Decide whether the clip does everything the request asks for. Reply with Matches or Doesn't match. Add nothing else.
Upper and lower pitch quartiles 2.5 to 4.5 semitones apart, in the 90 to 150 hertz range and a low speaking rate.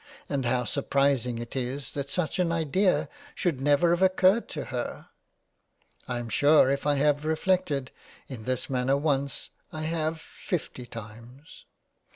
Doesn't match